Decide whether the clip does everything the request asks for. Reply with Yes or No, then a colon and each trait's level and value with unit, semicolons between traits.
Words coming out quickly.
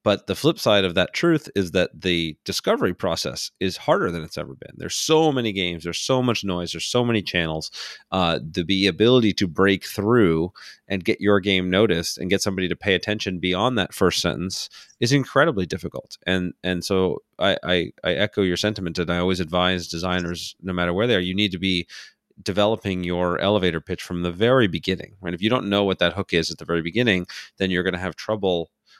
Yes: fast, 215 wpm